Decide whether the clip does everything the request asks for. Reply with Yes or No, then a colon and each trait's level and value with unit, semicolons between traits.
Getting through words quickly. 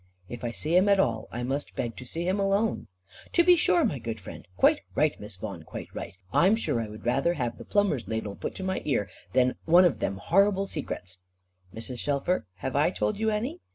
Yes: fast, 225 wpm